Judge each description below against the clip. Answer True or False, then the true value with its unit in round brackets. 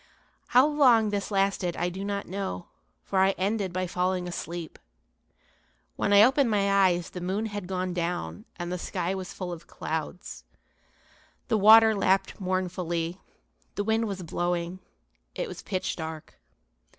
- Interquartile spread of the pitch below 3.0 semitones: True (2.5 semitones)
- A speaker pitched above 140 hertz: True (185 Hz)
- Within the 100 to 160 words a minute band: True (150 wpm)